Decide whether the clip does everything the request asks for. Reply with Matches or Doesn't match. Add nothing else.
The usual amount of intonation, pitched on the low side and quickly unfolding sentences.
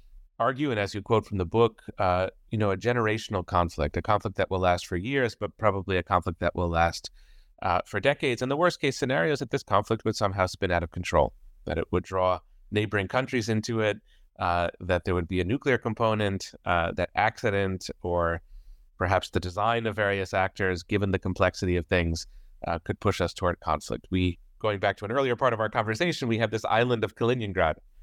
Matches